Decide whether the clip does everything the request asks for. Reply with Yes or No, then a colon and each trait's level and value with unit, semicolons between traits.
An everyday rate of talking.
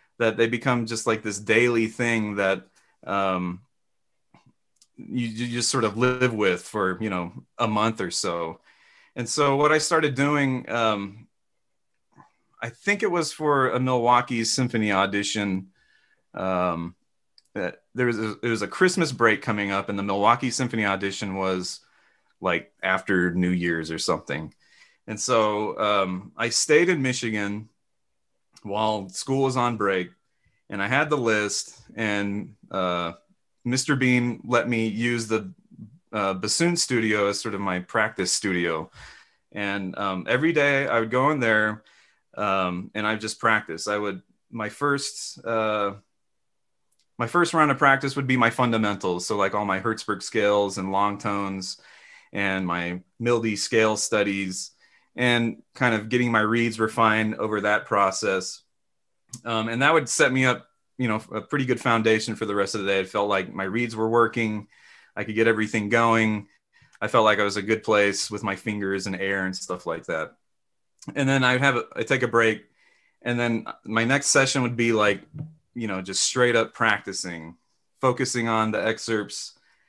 Yes: average, 170 wpm